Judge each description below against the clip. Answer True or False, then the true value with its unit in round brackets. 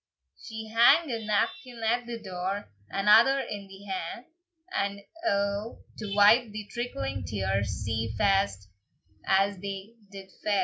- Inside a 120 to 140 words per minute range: True (135 wpm)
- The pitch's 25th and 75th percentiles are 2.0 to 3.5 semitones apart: True (2.9 semitones)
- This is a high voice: True (200 Hz)